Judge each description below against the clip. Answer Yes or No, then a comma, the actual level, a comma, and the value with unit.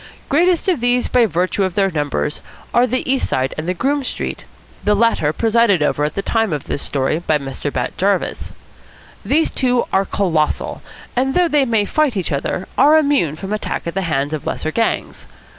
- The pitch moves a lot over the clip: Yes, wide, 8.3 semitones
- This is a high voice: Yes, high, 200 Hz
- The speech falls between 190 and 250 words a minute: Yes, average, 195 wpm